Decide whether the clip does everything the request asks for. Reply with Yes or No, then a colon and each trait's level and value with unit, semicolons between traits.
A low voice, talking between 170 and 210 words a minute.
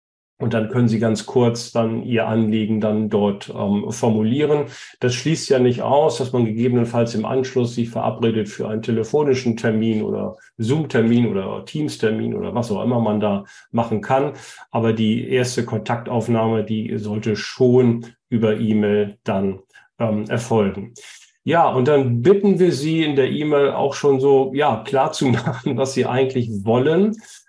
No: low, 120 Hz; average, 160 wpm